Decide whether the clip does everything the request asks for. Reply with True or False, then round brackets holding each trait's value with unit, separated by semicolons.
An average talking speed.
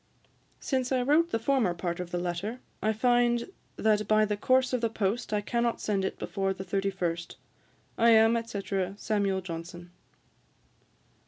True (165 wpm)